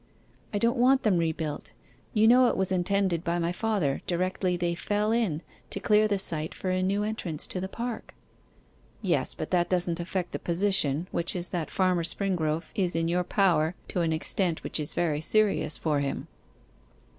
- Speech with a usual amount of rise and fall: Yes, average, 3.3 semitones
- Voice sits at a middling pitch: Yes, medium, 180 Hz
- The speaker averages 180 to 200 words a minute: Yes, average, 185 wpm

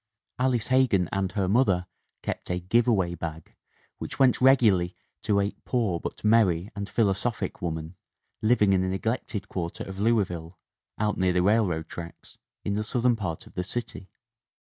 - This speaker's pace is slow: No, average, 170 wpm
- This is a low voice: Yes, low, 100 Hz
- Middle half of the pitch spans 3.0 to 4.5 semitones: Yes, average, 4.2 semitones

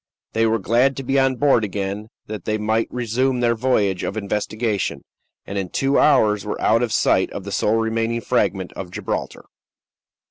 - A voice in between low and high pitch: No, low, 110 Hz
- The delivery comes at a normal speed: Yes, average, 180 wpm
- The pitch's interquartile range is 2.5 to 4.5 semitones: Yes, average, 2.8 semitones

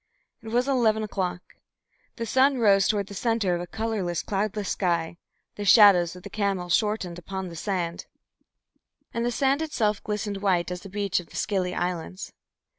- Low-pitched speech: No, high, 200 Hz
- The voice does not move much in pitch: No, average, 3.5 semitones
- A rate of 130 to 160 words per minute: No, average, 175 wpm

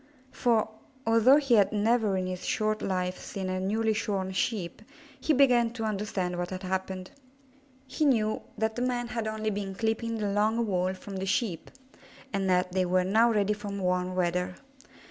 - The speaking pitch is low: No, high, 205 Hz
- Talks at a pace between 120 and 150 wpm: No, average, 180 wpm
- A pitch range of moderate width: Yes, average, 3.3 semitones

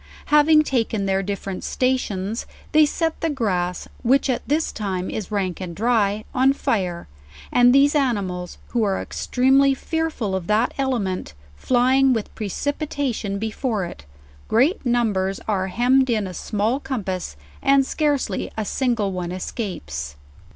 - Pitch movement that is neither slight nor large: No, wide, 5.7 semitones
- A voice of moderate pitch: No, high, 225 Hz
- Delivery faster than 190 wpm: No, average, 145 wpm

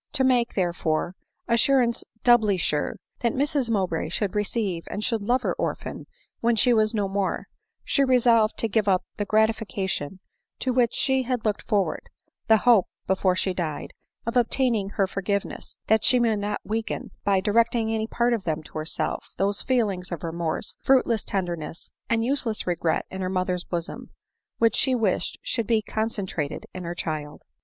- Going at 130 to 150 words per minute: No, average, 175 wpm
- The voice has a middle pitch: No, high, 210 Hz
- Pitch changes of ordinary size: Yes, average, 4.2 semitones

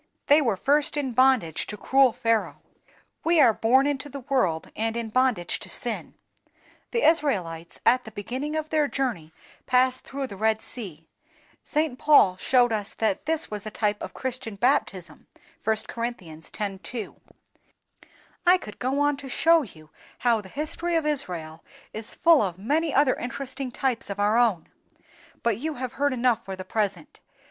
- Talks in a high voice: Yes, high, 245 Hz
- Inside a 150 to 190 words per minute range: Yes, average, 170 wpm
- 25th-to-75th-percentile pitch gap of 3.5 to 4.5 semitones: No, average, 5.3 semitones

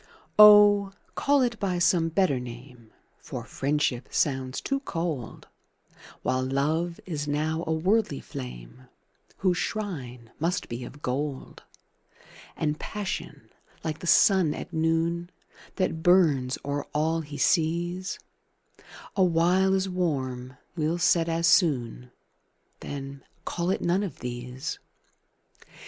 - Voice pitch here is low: No, medium, 160 Hz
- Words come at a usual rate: No, slow, 120 wpm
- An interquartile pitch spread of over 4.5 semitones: Yes, average, 5.2 semitones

